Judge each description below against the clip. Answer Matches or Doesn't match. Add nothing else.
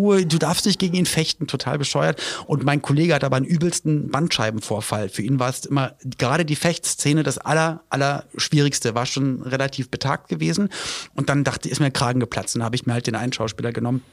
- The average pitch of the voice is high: Doesn't match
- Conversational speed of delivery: Doesn't match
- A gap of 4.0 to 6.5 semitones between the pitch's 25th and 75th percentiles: Matches